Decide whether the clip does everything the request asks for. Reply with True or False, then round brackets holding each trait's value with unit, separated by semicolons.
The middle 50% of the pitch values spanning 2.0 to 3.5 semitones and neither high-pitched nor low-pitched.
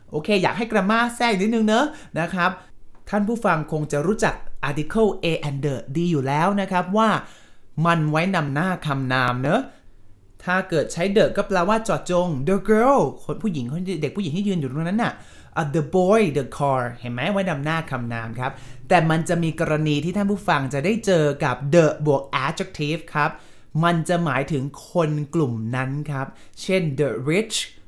False (5.1 semitones; 165 Hz)